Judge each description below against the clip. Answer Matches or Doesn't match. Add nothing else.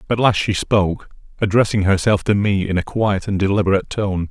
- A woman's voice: Doesn't match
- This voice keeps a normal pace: Matches